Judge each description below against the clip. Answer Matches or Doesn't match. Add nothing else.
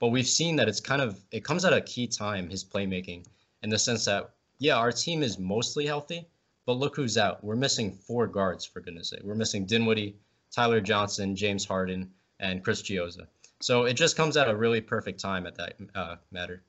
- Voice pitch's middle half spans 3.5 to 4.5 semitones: Matches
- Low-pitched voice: Matches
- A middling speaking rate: Doesn't match